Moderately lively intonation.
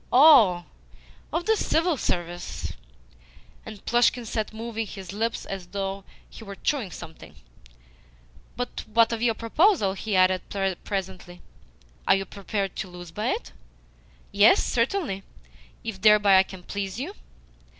Yes: average, 3.5 semitones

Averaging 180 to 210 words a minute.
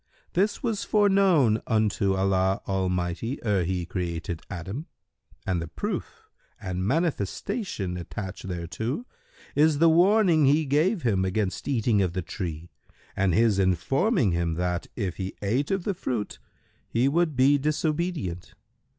No: slow, 135 wpm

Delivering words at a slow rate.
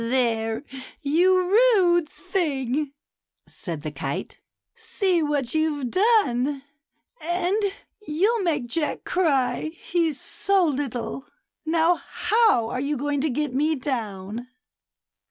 Yes: slow, 115 wpm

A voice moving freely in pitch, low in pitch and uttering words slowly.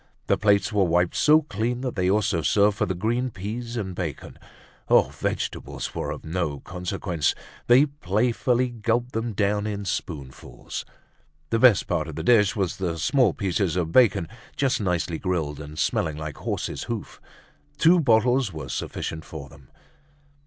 No: wide, 5.8 semitones; low, 100 Hz; average, 160 wpm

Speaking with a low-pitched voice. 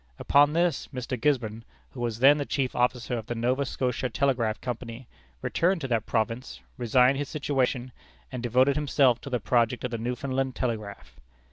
Yes: low, 125 Hz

